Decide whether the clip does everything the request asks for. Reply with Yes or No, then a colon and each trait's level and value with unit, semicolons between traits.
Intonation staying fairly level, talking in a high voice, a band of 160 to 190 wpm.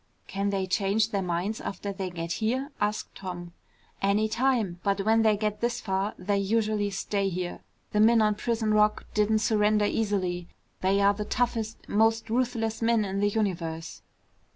Yes: narrow, 2.3 semitones; high, 210 Hz; average, 170 wpm